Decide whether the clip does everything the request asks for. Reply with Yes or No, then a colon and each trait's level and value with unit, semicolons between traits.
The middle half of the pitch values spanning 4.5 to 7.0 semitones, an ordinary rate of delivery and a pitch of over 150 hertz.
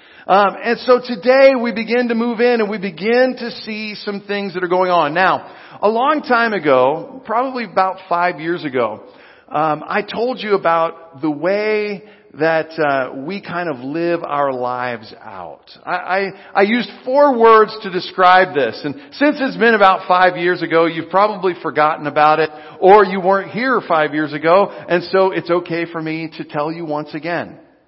Yes: average, 5.3 semitones; average, 185 wpm; medium, 185 Hz